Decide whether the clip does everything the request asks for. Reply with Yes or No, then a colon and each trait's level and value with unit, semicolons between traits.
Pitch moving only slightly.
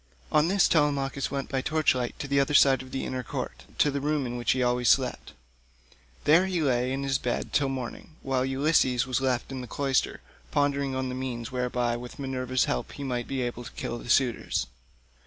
Yes: narrow, 2.1 semitones